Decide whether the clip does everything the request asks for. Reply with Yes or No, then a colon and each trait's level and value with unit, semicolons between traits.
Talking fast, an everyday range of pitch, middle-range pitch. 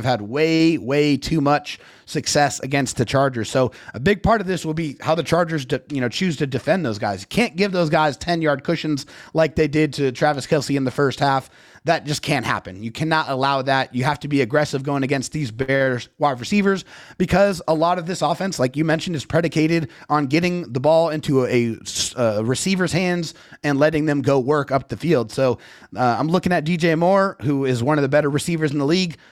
Yes: fast, 225 wpm; average, 3.5 semitones; medium, 150 Hz